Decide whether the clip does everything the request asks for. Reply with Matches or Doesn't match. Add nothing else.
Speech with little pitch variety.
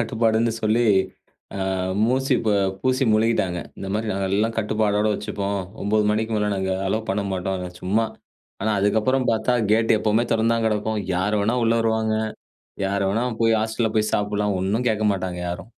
Matches